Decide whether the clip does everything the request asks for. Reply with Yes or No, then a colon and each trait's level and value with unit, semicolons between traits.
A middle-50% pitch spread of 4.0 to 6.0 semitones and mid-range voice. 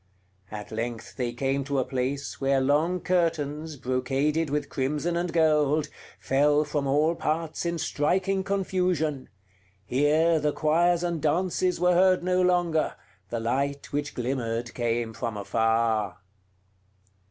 Yes: average, 4.5 semitones; medium, 145 Hz